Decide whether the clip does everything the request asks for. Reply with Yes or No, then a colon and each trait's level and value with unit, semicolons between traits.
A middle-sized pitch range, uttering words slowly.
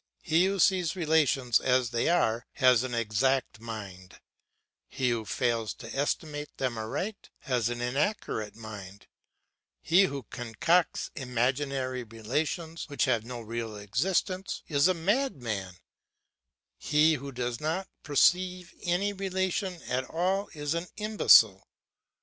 No: wide, 6.9 semitones; slow, 125 wpm